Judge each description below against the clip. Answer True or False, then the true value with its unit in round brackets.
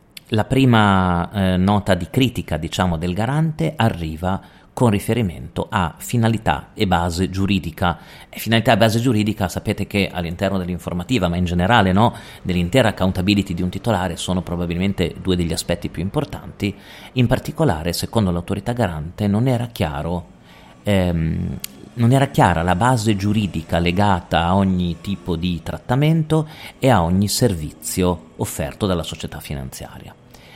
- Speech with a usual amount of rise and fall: True (4.4 semitones)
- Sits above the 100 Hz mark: False (95 Hz)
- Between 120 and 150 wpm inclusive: True (140 wpm)